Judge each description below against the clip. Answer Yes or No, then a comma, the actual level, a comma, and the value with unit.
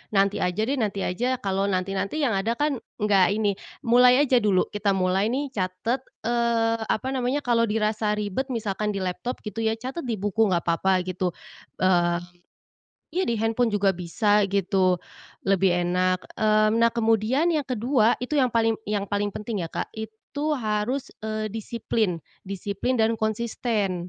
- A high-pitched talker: Yes, high, 215 Hz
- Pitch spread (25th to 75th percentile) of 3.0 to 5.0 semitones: Yes, average, 3.4 semitones